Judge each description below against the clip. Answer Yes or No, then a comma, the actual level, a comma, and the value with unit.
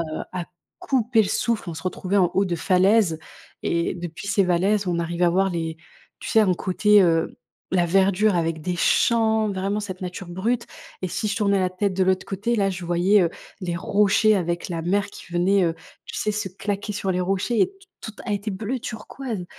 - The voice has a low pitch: No, high, 190 Hz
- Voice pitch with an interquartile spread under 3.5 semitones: Yes, average, 3.0 semitones